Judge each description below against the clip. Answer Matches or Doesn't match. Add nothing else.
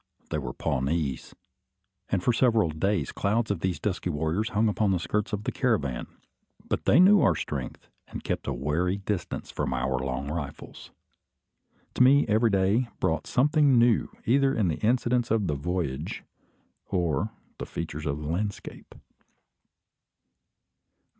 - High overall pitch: Doesn't match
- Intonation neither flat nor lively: Doesn't match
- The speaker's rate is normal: Matches